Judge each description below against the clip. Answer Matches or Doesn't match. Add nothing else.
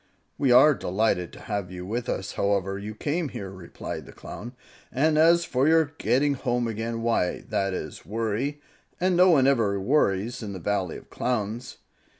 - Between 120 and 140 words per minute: Doesn't match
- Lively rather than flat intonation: Matches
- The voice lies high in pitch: Doesn't match